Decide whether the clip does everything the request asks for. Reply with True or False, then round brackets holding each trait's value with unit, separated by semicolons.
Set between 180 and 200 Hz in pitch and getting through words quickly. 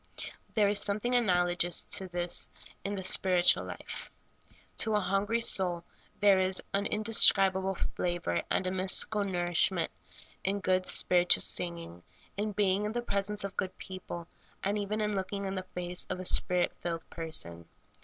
False (190 Hz; 165 wpm)